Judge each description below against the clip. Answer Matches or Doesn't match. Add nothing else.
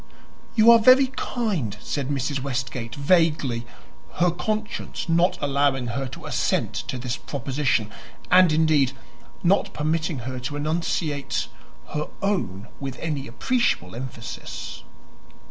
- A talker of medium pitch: Matches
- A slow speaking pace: Matches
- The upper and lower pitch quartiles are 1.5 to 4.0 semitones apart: Doesn't match